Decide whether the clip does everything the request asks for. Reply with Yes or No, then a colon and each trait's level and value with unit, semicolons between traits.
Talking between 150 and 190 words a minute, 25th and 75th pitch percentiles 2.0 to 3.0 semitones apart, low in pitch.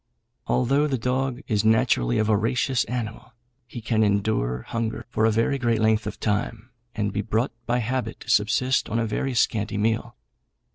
Yes: average, 175 wpm; narrow, 2.6 semitones; low, 110 Hz